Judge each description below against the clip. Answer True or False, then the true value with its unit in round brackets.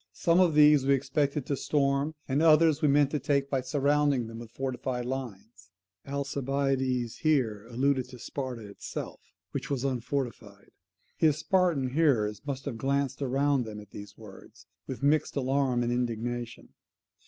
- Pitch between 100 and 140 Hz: True (135 Hz)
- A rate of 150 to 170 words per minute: True (155 wpm)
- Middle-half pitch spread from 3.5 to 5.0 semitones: False (2.7 semitones)